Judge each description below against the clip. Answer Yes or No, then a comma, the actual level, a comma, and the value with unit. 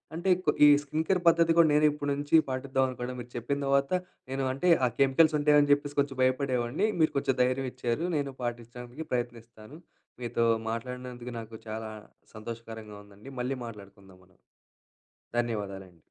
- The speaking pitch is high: No, low, 125 Hz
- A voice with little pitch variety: No, average, 3.7 semitones